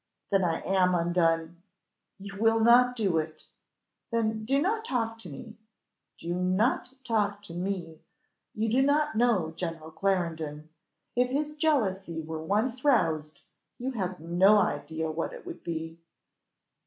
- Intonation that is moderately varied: No, wide, 5.9 semitones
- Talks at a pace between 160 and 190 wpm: No, average, 140 wpm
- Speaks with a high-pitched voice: Yes, high, 195 Hz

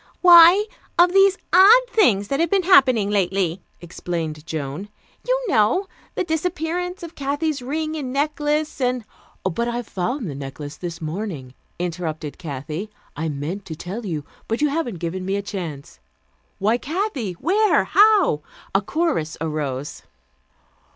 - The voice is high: Yes, high, 220 Hz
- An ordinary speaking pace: Yes, average, 145 wpm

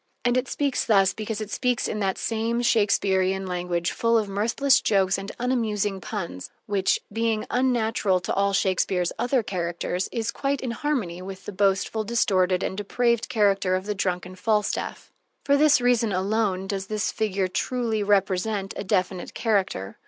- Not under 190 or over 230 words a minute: No, average, 160 wpm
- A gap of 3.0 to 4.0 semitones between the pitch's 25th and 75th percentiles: Yes, average, 3.4 semitones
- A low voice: No, high, 205 Hz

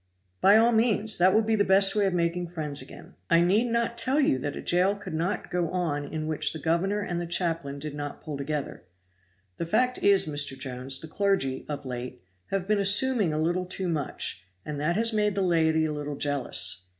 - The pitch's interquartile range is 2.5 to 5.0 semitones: No, wide, 5.4 semitones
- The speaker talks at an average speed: No, fast, 215 wpm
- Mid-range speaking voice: Yes, medium, 170 Hz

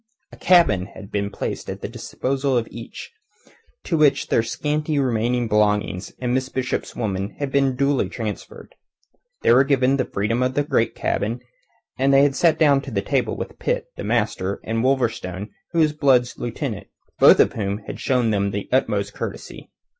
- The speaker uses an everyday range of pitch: Yes, average, 4.7 semitones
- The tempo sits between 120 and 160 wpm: No, average, 175 wpm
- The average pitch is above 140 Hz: No, low, 125 Hz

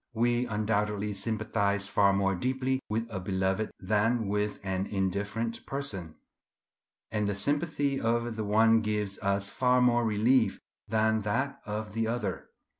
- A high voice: No, low, 110 Hz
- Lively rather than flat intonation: No, average, 2.7 semitones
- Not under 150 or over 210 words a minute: No, average, 140 wpm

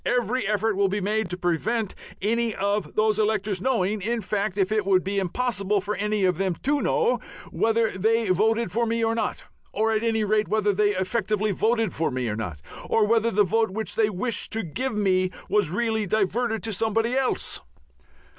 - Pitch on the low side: No, high, 215 Hz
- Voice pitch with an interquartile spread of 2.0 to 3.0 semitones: Yes, narrow, 2.6 semitones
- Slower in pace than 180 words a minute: No, average, 195 wpm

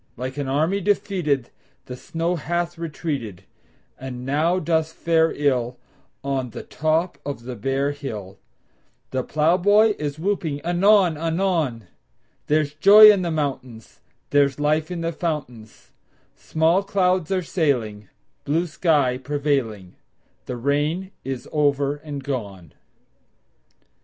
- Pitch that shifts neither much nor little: Yes, average, 4.3 semitones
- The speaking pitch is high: No, medium, 150 Hz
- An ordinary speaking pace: No, slow, 120 wpm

